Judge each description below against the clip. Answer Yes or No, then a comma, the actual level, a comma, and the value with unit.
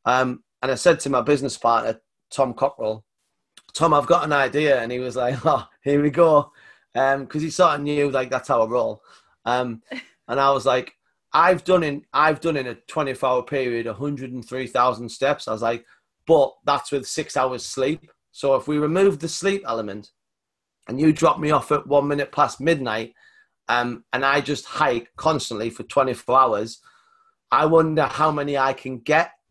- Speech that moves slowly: No, average, 200 wpm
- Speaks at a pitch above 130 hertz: Yes, medium, 140 Hz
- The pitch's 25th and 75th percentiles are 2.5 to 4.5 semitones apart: Yes, average, 4.0 semitones